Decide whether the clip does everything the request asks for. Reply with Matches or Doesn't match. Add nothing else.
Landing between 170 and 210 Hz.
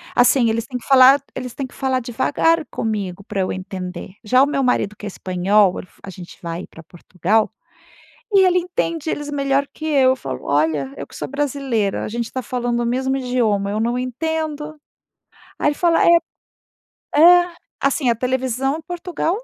Doesn't match